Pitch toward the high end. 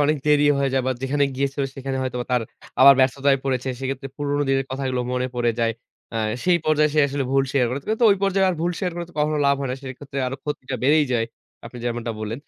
No: low, 135 Hz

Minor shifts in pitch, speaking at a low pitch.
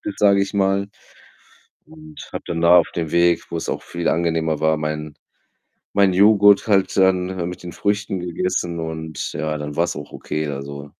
No: average, 3.8 semitones; very low, 85 Hz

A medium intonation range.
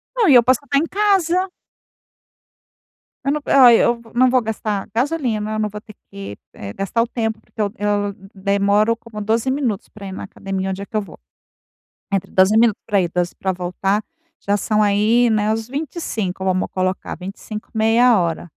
Yes: average, 3.4 semitones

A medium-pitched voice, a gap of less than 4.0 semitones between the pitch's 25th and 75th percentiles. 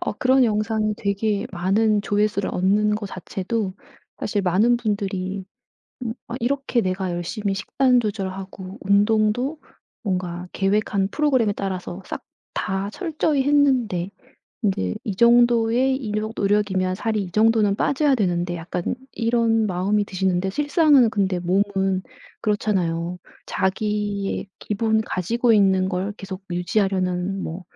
No: high, 205 Hz; average, 3.1 semitones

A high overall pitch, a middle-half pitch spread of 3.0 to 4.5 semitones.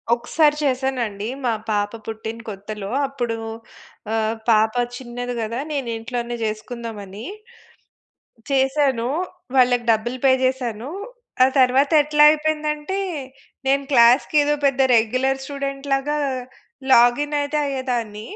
Yes: very high, 250 Hz; average, 3.5 semitones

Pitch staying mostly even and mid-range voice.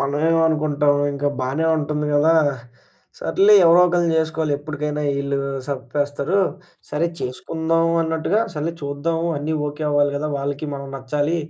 Yes: narrow, 2.2 semitones; medium, 150 Hz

